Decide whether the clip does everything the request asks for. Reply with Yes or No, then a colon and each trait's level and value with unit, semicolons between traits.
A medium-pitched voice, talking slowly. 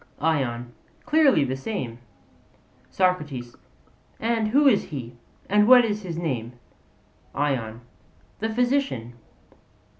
Yes: medium, 165 Hz; slow, 100 wpm